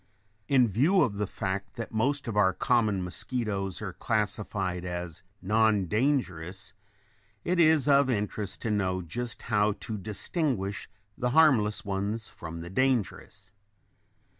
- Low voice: Yes, low, 105 Hz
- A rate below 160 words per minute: Yes, average, 140 wpm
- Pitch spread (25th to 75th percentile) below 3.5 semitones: No, average, 4.3 semitones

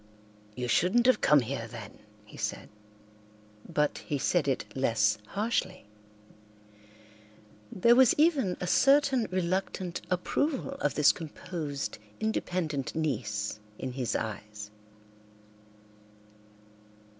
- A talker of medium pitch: Yes, medium, 160 Hz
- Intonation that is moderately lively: No, wide, 7.9 semitones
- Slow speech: Yes, slow, 100 wpm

